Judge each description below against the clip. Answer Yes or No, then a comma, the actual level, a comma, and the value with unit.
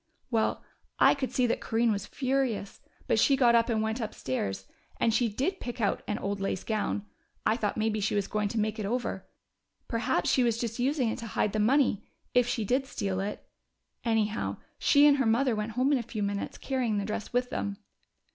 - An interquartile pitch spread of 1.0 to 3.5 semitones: Yes, average, 3.1 semitones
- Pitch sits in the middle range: No, high, 225 Hz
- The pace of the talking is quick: Yes, fast, 215 wpm